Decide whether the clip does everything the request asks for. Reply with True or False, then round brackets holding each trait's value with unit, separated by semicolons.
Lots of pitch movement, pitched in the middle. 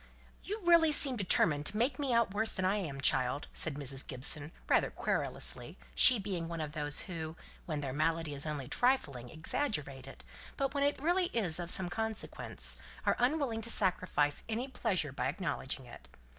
True (8.2 semitones; 175 Hz)